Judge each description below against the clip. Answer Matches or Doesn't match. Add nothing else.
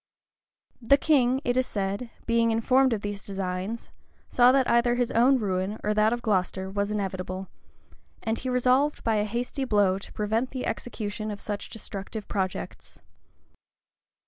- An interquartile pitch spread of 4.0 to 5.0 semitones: Doesn't match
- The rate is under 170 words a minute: Matches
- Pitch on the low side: Doesn't match